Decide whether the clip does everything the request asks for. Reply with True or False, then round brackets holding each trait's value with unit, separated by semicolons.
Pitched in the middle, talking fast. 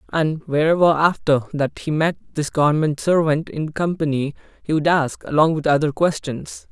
False (155 Hz; 160 wpm)